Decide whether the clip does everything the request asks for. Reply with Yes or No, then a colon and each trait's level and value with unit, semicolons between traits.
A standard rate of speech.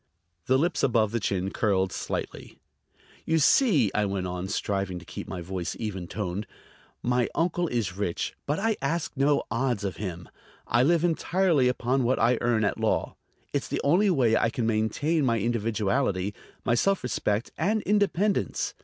Yes: average, 170 wpm